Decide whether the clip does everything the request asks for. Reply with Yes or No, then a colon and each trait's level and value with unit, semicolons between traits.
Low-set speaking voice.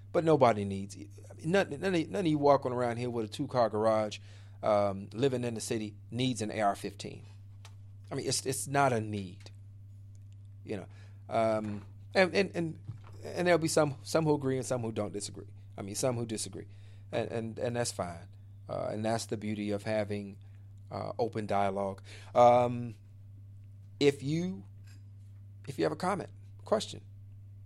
Yes: low, 105 Hz